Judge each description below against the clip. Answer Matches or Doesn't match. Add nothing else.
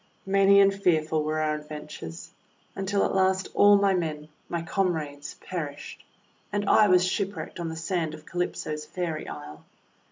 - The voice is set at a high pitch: Doesn't match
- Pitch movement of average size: Matches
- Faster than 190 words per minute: Doesn't match